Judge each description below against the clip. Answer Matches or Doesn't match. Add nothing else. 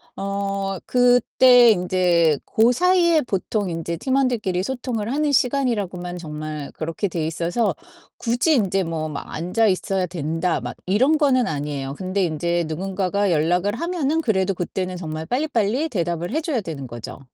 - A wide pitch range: Matches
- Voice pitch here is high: Matches